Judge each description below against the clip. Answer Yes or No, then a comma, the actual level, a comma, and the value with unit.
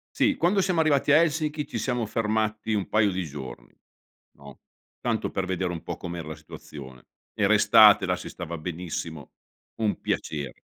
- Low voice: Yes, very low, 95 Hz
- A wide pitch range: Yes, wide, 8.8 semitones